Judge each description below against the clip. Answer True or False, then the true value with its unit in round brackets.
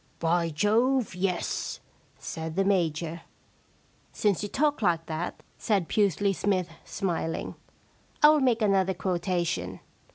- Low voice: False (185 Hz)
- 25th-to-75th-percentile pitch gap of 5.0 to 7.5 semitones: False (3.7 semitones)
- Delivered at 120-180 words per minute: True (135 wpm)